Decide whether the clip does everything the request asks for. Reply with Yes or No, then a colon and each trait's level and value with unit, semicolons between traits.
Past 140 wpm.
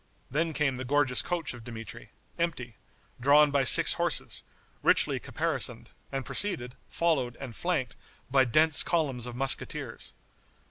No: slow, 135 wpm